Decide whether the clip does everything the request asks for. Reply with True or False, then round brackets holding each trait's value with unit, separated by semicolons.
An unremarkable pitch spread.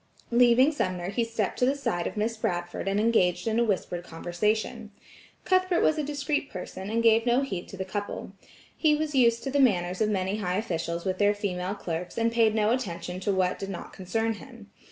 True (4.2 semitones)